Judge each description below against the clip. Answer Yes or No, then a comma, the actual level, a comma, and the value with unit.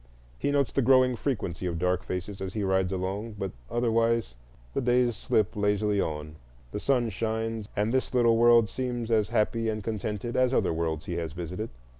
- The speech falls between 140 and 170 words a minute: No, average, 180 wpm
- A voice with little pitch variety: No, average, 4.0 semitones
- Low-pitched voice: Yes, low, 110 Hz